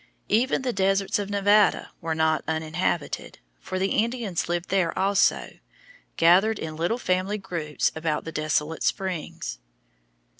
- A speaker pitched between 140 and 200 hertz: Yes, medium, 185 Hz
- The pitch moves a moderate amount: Yes, average, 3.9 semitones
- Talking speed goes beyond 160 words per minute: No, slow, 135 wpm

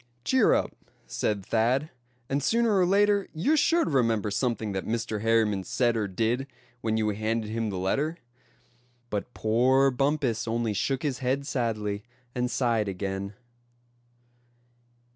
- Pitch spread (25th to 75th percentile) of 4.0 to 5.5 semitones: Yes, average, 4.3 semitones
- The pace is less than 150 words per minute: Yes, average, 140 wpm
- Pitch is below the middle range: Yes, low, 115 Hz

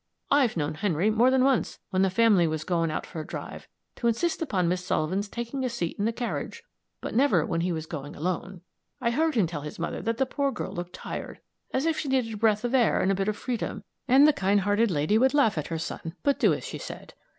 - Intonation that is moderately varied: No, wide, 6.4 semitones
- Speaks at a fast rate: Yes, fast, 250 wpm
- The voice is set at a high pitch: Yes, high, 205 Hz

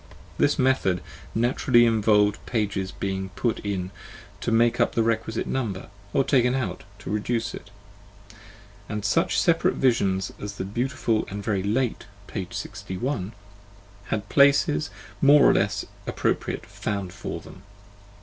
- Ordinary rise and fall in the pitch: Yes, average, 3.8 semitones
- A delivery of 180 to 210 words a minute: No, slow, 135 wpm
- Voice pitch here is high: No, low, 110 Hz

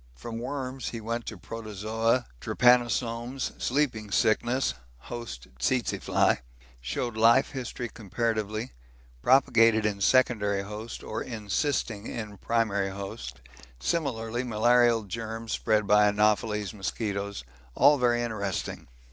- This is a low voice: Yes, low, 115 Hz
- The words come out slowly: Yes, slow, 110 wpm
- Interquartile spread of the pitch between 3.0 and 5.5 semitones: No, narrow, 2.6 semitones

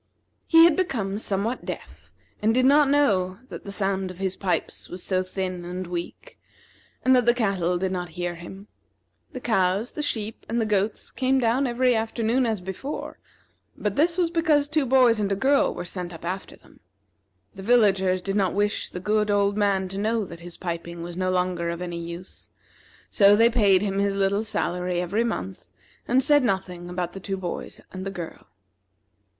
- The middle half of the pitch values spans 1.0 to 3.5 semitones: No, average, 4.2 semitones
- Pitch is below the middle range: No, high, 195 Hz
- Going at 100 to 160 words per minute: No, average, 190 wpm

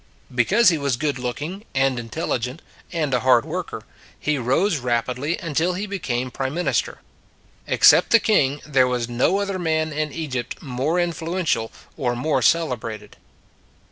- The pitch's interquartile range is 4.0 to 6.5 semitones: Yes, average, 5.1 semitones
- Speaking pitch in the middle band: Yes, medium, 145 Hz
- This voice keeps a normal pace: Yes, average, 150 wpm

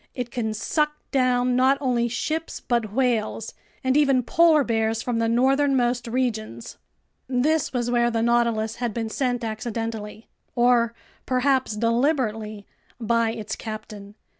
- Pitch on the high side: Yes, high, 240 Hz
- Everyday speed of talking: No, slow, 125 wpm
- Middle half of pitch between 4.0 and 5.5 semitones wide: No, narrow, 2.4 semitones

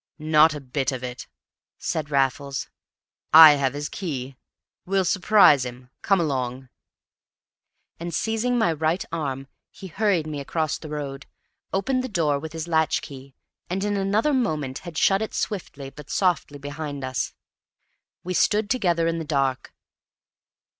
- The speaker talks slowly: No, average, 150 wpm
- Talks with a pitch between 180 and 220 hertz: No, medium, 155 Hz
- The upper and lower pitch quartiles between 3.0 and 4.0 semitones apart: No, average, 5.1 semitones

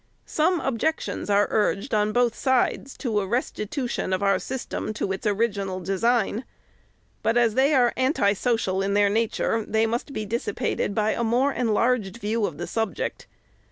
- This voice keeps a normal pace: Yes, average, 170 wpm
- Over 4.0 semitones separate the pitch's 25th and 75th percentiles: No, average, 3.3 semitones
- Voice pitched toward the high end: Yes, high, 225 Hz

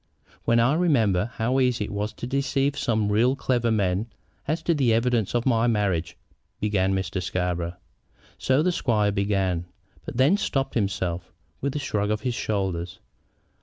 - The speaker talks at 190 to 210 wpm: No, average, 165 wpm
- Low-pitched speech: Yes, low, 110 Hz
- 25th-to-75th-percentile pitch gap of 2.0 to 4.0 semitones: No, average, 5.0 semitones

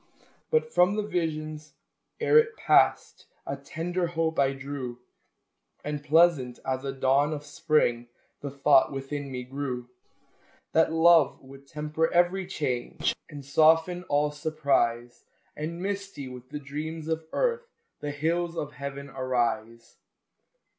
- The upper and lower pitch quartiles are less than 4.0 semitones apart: Yes, average, 3.3 semitones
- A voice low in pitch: No, medium, 150 Hz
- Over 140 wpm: No, slow, 135 wpm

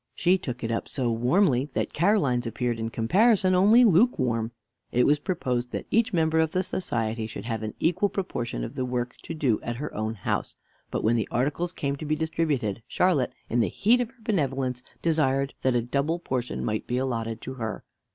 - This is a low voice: Yes, low, 130 Hz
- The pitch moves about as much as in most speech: No, wide, 6.4 semitones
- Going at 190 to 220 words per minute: Yes, average, 200 wpm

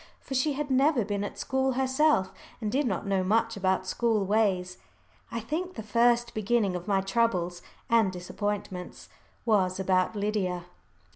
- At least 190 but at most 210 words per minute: No, average, 155 wpm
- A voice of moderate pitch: No, high, 210 Hz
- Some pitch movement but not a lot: Yes, average, 4.2 semitones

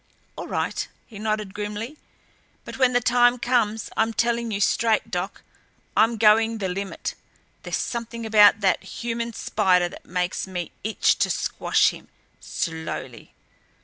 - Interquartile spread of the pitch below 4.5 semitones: Yes, average, 2.9 semitones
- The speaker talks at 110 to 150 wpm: Yes, average, 145 wpm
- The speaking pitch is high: Yes, high, 220 Hz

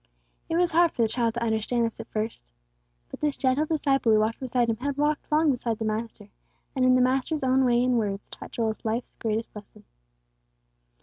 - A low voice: No, high, 245 Hz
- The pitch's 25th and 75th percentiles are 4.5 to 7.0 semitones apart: No, average, 3.4 semitones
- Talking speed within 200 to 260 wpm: Yes, fast, 205 wpm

